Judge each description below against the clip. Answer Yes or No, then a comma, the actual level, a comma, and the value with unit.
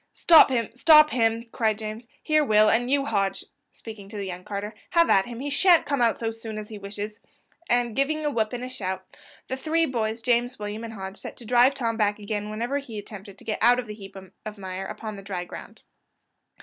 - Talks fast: Yes, fast, 230 wpm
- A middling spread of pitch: Yes, average, 3.2 semitones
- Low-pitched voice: No, high, 225 Hz